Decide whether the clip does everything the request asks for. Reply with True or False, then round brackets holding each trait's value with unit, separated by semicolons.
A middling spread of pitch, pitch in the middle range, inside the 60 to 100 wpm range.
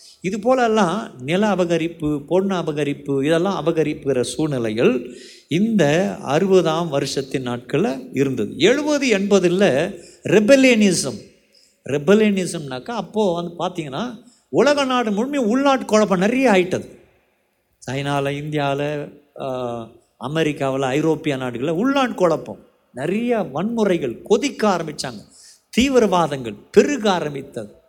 False (7.1 semitones; 175 Hz; 90 wpm)